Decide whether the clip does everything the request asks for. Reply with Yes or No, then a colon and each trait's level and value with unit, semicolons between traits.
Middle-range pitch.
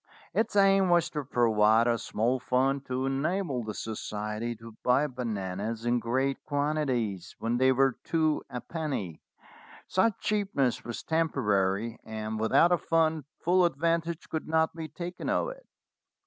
No: low, 130 Hz